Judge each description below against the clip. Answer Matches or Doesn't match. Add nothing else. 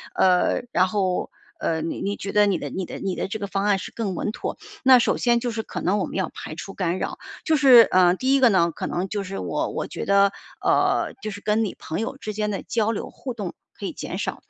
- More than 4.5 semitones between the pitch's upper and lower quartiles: Doesn't match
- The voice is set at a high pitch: Matches